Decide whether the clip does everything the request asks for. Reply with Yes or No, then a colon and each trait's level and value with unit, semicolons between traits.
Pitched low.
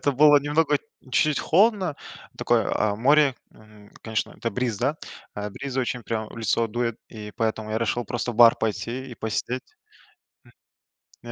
Yes: low, 120 Hz